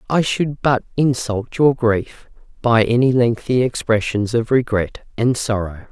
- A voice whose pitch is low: Yes, low, 120 Hz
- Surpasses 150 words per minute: No, average, 140 wpm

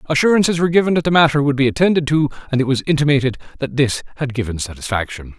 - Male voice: Yes, male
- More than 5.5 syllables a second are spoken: Yes, 7.5 syllables/s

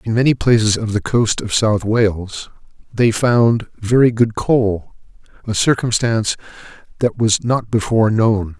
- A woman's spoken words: No, male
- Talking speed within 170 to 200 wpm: No, average, 145 wpm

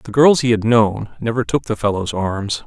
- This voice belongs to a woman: No, male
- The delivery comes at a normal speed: No, fast, 225 wpm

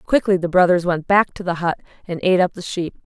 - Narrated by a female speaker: Yes, female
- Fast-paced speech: Yes, fast, 255 wpm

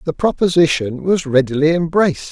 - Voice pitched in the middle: Yes, medium, 160 Hz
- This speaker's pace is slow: Yes, slow, 130 wpm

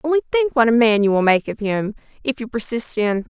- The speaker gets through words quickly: Yes, fast, 250 wpm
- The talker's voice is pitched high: Yes, high, 235 Hz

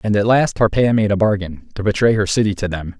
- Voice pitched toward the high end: No, low, 105 Hz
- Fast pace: Yes, fast, 260 wpm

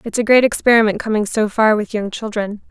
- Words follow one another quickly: Yes, fast, 220 wpm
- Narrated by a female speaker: Yes, female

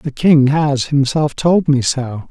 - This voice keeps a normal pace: Yes, average, 180 wpm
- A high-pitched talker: No, medium, 140 Hz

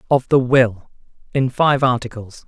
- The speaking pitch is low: Yes, low, 125 Hz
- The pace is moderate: Yes, average, 145 wpm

